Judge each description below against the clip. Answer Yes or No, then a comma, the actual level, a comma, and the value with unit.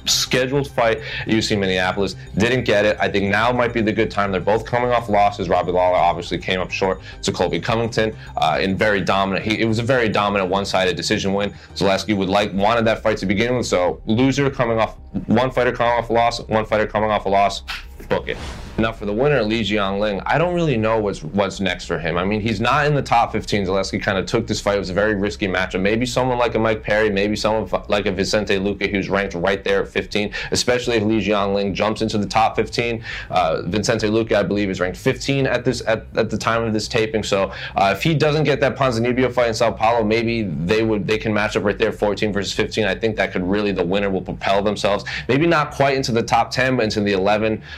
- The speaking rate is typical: No, fast, 245 wpm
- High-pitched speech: No, low, 110 Hz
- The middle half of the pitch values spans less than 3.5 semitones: Yes, average, 2.7 semitones